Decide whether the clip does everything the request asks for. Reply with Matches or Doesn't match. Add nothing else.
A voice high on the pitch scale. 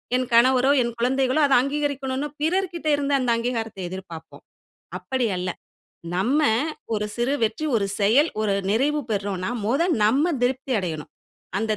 Matches